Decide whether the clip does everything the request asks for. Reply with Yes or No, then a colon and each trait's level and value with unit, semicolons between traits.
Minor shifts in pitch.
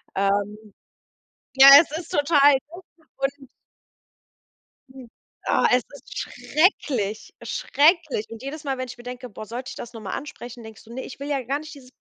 No: average, 3.8 semitones